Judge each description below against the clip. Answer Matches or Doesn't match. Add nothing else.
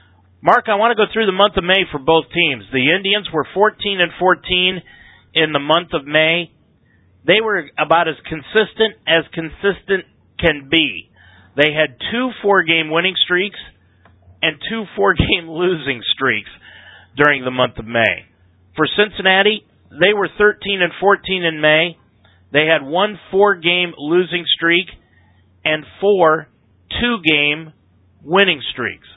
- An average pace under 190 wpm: Matches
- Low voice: Doesn't match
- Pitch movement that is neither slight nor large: Doesn't match